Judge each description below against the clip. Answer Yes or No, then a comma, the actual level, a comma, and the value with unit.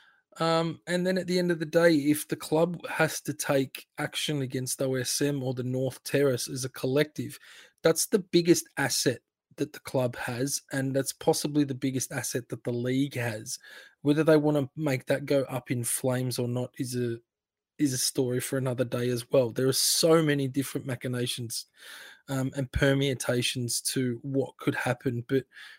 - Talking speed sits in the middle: Yes, average, 185 wpm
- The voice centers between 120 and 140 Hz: Yes, low, 135 Hz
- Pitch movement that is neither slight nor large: Yes, average, 3.0 semitones